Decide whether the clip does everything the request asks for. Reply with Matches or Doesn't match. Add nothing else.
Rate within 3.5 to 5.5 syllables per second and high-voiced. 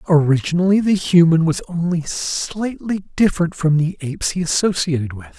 Doesn't match